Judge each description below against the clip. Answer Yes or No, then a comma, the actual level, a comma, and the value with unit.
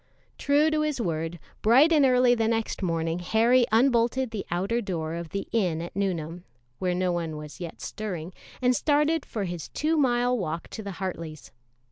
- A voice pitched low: No, high, 200 Hz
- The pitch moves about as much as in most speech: No, wide, 6.5 semitones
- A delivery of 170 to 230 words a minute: Yes, average, 180 wpm